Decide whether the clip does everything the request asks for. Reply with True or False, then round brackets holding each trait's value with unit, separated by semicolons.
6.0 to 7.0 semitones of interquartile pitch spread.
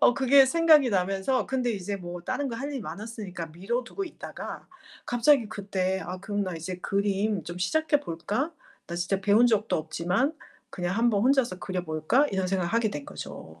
False (5.5 semitones)